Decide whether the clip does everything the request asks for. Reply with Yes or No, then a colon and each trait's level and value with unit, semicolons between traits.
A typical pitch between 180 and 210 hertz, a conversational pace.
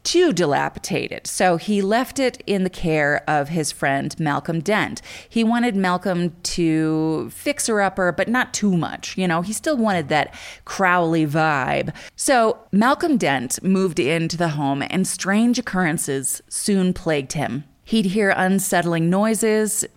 Yes: medium, 185 Hz; average, 150 wpm